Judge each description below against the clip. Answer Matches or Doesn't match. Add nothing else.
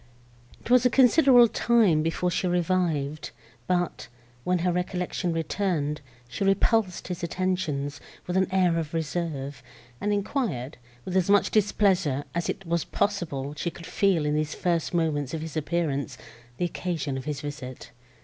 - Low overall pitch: Doesn't match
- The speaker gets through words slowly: Doesn't match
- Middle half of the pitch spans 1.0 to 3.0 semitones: Doesn't match